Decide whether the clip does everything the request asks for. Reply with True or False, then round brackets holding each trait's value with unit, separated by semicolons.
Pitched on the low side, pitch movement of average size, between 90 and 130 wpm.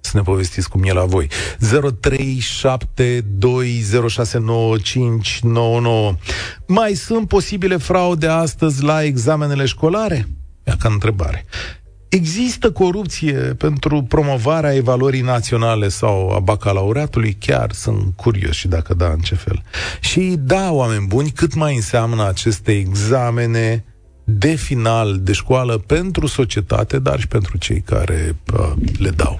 False (115 Hz; 6.4 semitones; 120 wpm)